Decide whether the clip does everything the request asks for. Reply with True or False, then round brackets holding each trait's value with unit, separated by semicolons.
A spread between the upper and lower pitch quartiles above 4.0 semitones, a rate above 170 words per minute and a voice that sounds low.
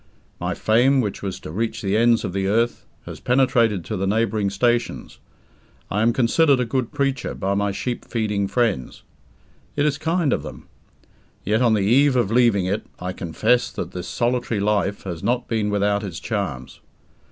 False (3.7 semitones; 180 wpm; 110 Hz)